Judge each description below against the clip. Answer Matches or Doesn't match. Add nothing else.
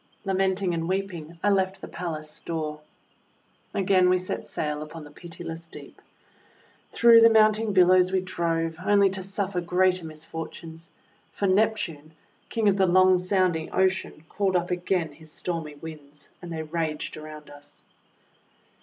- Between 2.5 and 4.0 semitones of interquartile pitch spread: Matches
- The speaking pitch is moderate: Matches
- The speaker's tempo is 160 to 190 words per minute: Doesn't match